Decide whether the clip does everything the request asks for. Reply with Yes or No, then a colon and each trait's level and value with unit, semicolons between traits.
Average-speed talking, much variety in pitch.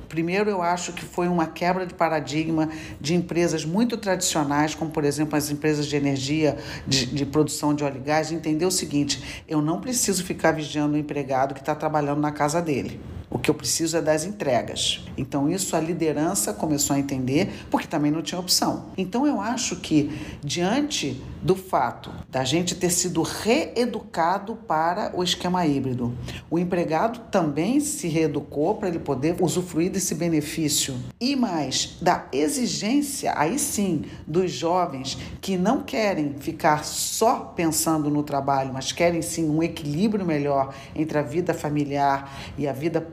No: average, 165 wpm; average, 3.6 semitones